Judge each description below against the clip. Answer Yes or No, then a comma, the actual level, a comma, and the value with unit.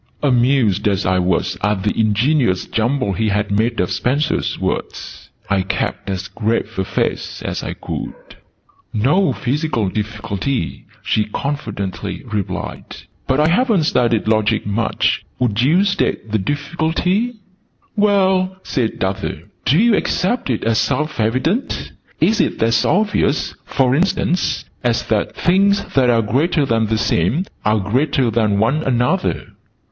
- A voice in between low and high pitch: No, low, 120 Hz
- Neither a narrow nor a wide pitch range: No, wide, 6.7 semitones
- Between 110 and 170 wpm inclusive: Yes, average, 140 wpm